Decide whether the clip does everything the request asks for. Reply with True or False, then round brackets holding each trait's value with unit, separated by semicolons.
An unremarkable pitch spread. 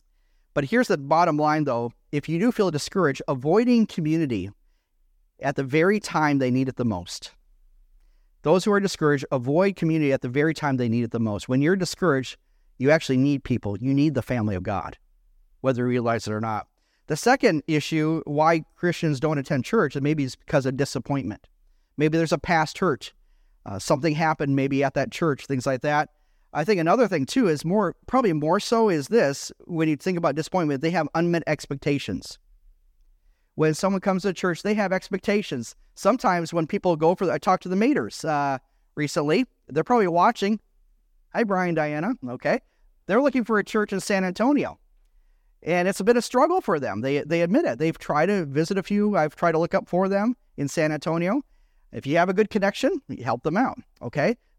False (5.7 semitones)